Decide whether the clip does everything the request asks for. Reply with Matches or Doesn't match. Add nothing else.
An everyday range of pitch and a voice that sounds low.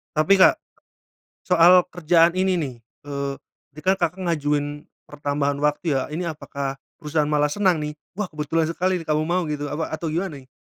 Doesn't match